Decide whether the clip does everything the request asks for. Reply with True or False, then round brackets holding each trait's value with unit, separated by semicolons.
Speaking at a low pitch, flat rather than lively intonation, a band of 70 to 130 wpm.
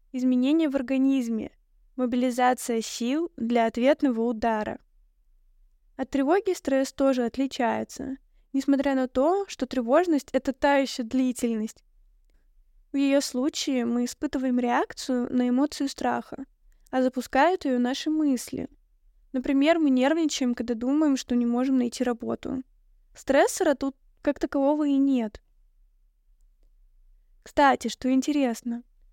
False (265 Hz; 2.3 semitones; 115 wpm)